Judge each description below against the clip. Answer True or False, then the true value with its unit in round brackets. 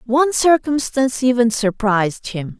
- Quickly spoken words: False (115 wpm)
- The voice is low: False (245 Hz)